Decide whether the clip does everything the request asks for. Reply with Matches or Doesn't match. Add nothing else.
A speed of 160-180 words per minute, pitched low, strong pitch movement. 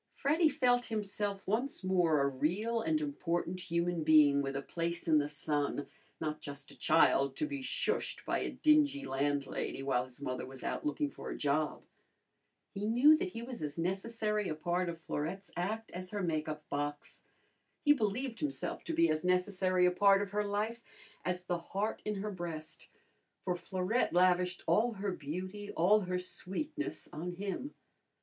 Doesn't match